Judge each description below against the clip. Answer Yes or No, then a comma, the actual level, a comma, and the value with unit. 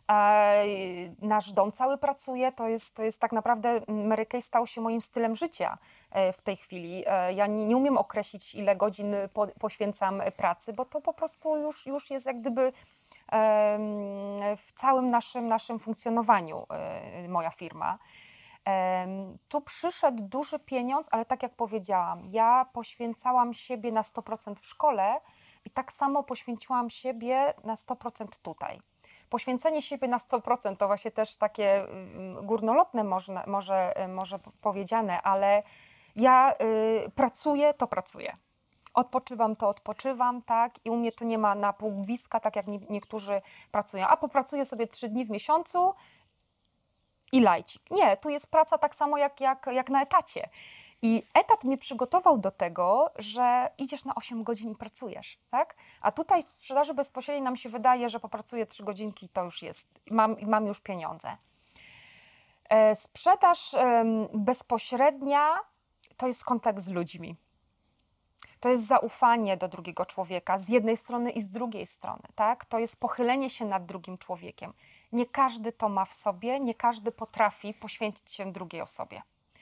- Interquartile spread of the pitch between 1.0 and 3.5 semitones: No, average, 3.9 semitones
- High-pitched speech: Yes, high, 230 Hz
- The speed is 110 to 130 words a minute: No, average, 150 wpm